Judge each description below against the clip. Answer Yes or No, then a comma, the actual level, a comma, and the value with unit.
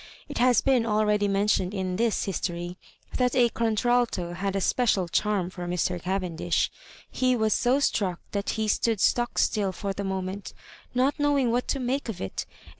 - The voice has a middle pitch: No, high, 210 Hz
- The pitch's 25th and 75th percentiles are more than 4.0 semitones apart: Yes, average, 4.5 semitones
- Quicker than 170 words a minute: Yes, average, 185 wpm